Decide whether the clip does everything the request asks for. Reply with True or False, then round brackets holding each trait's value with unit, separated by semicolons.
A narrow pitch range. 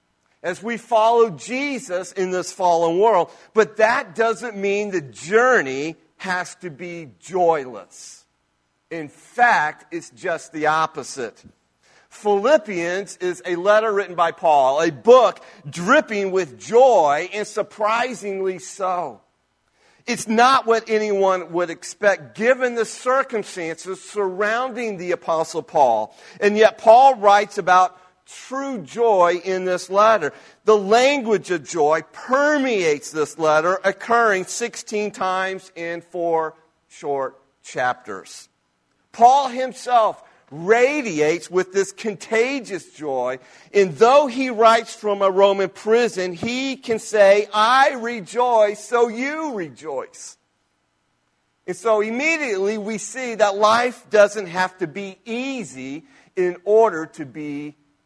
False (5.1 semitones)